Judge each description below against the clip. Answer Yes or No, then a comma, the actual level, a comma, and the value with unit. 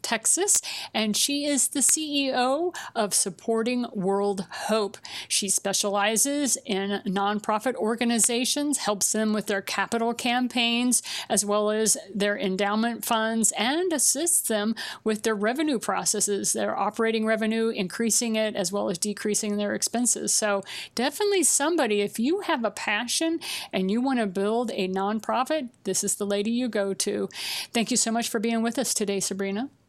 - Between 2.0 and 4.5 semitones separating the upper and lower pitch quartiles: Yes, average, 3.3 semitones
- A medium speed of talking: Yes, average, 155 wpm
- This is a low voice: No, high, 220 Hz